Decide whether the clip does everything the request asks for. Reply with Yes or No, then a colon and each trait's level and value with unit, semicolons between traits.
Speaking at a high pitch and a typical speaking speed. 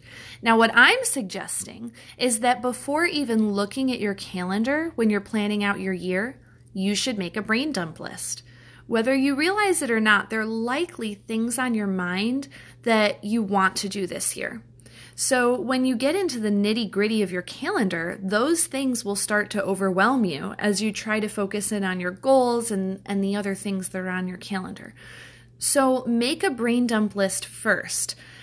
Yes: high, 210 Hz; average, 190 wpm